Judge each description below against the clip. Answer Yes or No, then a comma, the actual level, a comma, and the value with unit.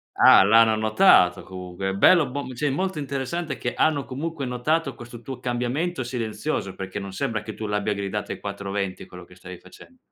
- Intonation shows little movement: No, wide, 5.9 semitones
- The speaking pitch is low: Yes, low, 120 Hz